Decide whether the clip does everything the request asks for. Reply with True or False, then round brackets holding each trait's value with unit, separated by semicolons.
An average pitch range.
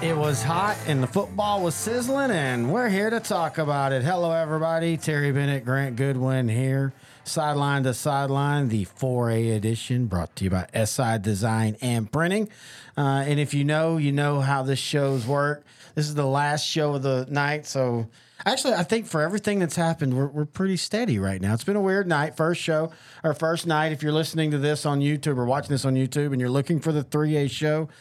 True (3.4 semitones)